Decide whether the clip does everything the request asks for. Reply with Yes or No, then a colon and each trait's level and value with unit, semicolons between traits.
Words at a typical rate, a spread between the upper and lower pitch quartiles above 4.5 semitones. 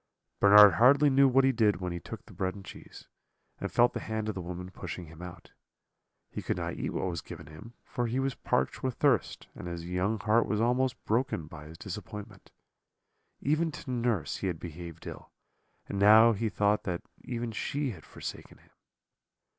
Yes: average, 195 wpm; average, 5.2 semitones